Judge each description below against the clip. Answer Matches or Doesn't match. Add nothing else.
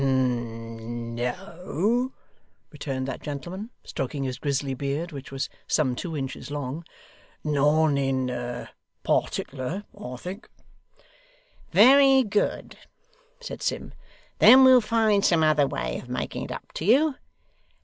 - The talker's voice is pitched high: Doesn't match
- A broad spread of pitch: Matches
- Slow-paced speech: Matches